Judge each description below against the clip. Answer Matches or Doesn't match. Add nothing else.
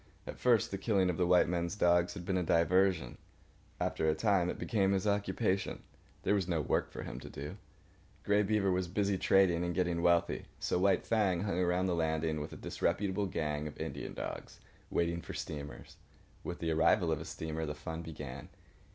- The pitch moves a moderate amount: Matches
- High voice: Doesn't match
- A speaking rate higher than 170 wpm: Matches